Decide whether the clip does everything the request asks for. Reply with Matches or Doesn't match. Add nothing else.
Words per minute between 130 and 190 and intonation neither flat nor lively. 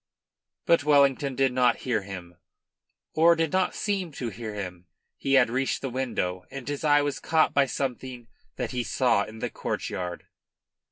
Matches